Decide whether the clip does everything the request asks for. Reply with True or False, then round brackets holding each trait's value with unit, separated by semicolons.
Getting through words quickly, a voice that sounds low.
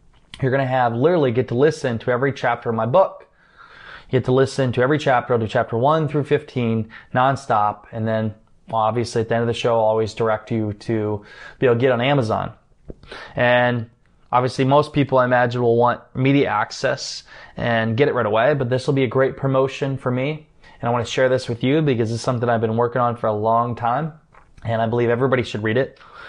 True (225 wpm; 120 Hz)